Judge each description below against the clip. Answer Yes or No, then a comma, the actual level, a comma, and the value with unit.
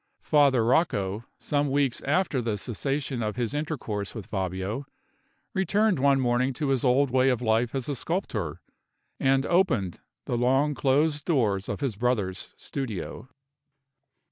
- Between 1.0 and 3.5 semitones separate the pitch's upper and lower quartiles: No, average, 4.1 semitones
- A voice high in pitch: No, low, 130 Hz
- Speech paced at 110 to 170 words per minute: Yes, average, 140 wpm